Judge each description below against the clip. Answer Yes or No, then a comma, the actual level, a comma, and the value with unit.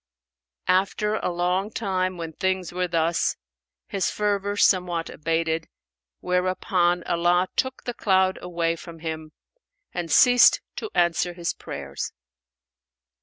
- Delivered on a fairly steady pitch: Yes, narrow, 2.0 semitones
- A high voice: No, medium, 180 Hz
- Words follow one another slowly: Yes, slow, 120 wpm